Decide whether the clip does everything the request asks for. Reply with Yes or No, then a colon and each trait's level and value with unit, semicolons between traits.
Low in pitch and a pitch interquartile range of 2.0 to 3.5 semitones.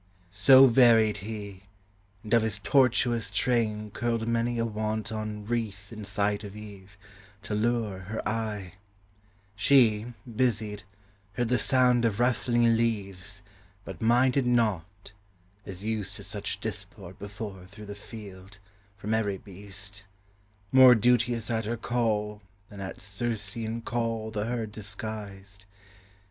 Yes: low, 110 Hz; narrow, 2.4 semitones